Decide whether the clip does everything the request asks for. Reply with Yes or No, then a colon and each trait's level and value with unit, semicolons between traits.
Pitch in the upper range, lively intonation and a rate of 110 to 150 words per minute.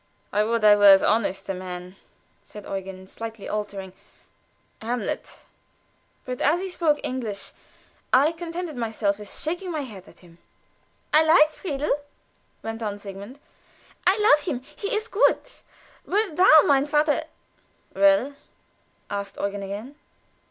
Yes: high, 230 Hz; wide, 7.3 semitones; average, 140 wpm